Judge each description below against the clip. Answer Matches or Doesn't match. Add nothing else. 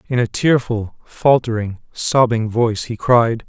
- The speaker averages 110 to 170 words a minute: Matches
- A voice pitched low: Matches